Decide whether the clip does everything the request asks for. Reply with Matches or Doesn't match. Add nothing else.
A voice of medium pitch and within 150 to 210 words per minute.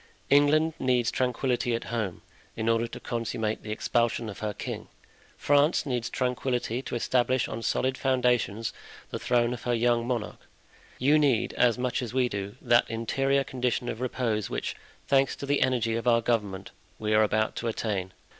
Doesn't match